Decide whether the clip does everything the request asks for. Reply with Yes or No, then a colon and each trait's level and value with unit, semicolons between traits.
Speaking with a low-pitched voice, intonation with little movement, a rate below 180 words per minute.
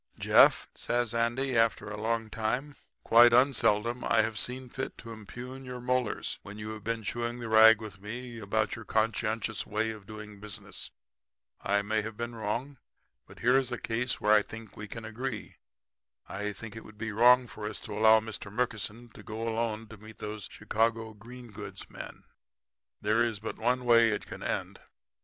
No: low, 110 Hz; narrow, 2.0 semitones; average, 195 wpm